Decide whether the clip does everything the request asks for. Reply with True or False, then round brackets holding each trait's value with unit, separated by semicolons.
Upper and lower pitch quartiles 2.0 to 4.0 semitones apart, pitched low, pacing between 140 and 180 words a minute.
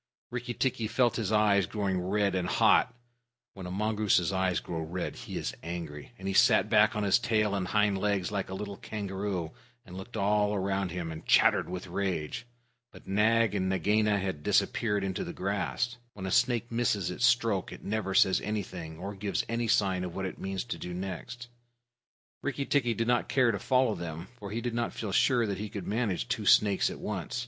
False (3.1 semitones; 100 Hz; 205 wpm)